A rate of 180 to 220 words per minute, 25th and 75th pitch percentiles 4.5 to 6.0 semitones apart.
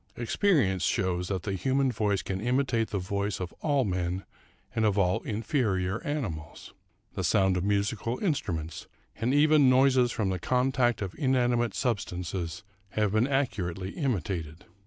No: average, 150 wpm; wide, 5.5 semitones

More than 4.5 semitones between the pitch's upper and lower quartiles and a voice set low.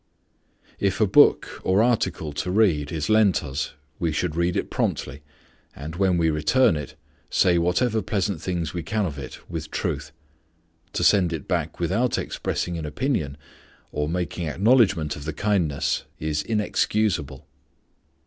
Yes: average, 4.9 semitones; very low, 85 Hz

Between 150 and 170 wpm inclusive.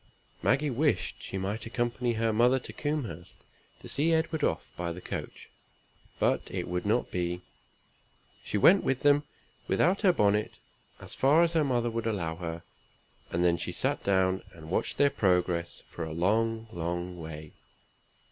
Yes: average, 165 wpm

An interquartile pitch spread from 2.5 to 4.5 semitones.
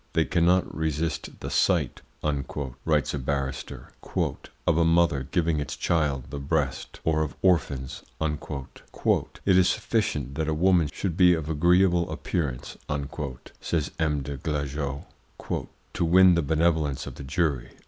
Yes: average, 3.3 semitones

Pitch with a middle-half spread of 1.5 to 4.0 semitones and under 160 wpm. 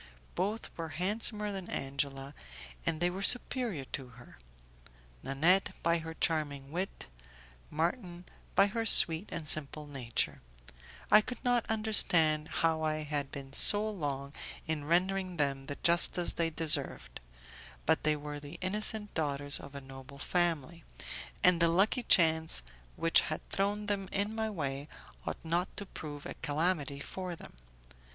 No: average, 5.0 semitones; average, 145 wpm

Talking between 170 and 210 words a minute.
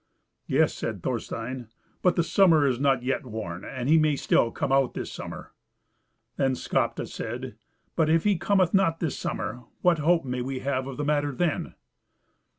Yes: average, 175 wpm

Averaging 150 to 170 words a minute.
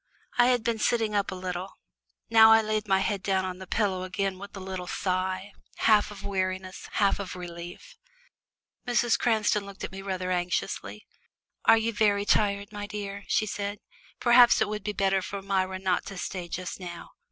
No: average, 185 wpm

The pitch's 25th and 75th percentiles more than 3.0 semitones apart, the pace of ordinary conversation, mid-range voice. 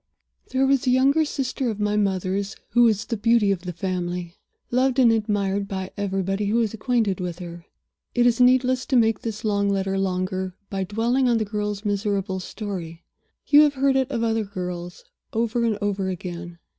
No: average, 3.9 semitones; average, 185 wpm; high, 205 Hz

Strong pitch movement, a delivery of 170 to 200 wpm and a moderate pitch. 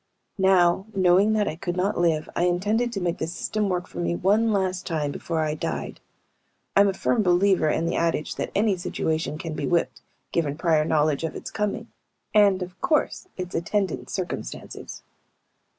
No: average, 3.5 semitones; average, 180 wpm; medium, 180 Hz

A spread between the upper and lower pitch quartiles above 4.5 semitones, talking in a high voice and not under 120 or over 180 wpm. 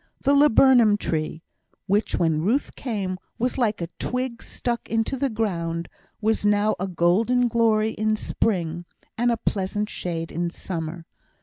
Yes: average, 5.1 semitones; high, 210 Hz; average, 145 wpm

